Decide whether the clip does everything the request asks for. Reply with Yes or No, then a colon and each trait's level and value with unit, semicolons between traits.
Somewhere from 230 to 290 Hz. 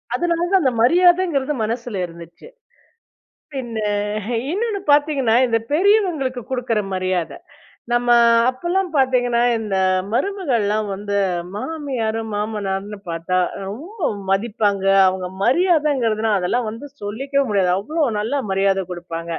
Yes: high, 240 Hz